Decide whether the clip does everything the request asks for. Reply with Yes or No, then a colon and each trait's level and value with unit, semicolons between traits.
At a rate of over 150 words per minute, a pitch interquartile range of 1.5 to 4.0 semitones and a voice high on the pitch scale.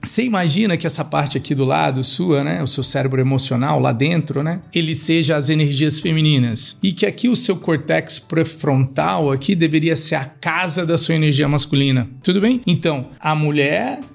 No: average, 180 wpm; average, 3.4 semitones; medium, 155 Hz